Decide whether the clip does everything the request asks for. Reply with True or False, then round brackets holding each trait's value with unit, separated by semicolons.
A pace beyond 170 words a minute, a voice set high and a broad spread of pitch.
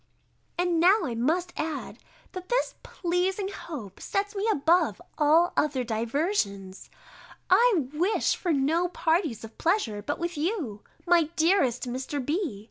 False (135 wpm; 325 Hz; 5.9 semitones)